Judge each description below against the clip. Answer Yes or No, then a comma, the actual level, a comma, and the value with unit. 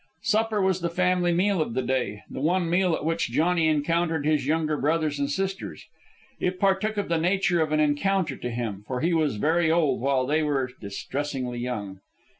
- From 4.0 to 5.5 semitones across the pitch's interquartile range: Yes, average, 4.7 semitones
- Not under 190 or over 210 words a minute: Yes, average, 195 wpm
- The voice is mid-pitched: Yes, medium, 160 Hz